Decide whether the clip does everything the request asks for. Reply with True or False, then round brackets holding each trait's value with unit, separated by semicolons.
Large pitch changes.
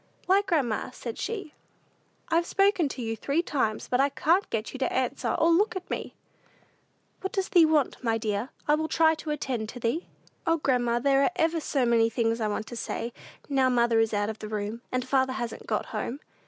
True (5.7 semitones)